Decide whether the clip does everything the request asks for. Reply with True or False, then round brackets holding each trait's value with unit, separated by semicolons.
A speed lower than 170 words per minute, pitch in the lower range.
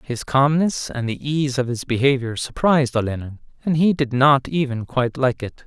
False (190 wpm; 130 Hz)